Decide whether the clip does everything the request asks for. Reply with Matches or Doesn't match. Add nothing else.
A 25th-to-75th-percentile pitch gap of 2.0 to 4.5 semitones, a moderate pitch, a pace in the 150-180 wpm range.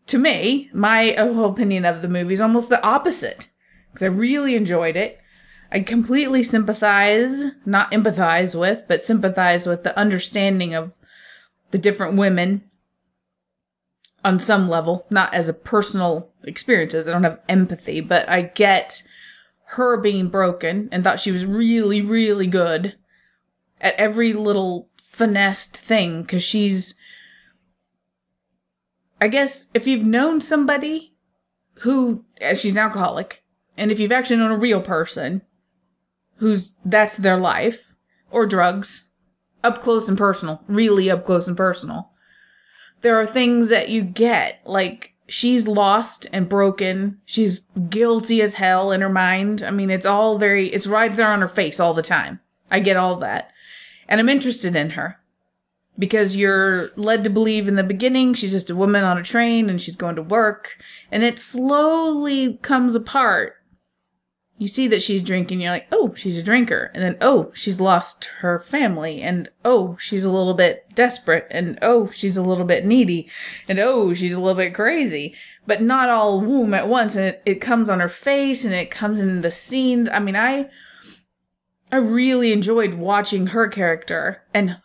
Doesn't match